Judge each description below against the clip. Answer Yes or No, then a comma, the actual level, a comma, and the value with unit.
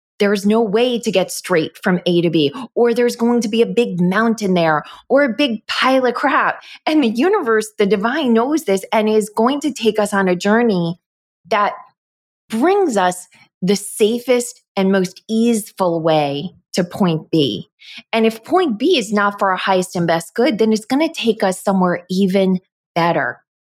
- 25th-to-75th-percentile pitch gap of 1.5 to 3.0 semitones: No, average, 4.2 semitones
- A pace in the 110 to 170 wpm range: No, average, 190 wpm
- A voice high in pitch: Yes, high, 215 Hz